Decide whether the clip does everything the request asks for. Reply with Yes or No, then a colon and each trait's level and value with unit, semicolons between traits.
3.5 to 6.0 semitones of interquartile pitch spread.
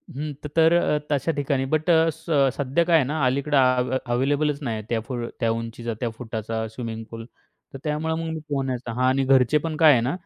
Yes: average, 4.0 semitones